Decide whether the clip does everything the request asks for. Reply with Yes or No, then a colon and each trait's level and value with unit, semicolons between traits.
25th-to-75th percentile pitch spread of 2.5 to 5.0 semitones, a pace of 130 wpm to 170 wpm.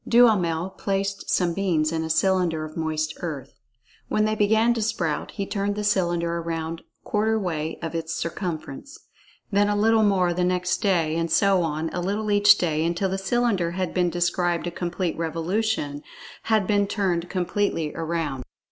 Yes: average, 3.7 semitones; average, 165 wpm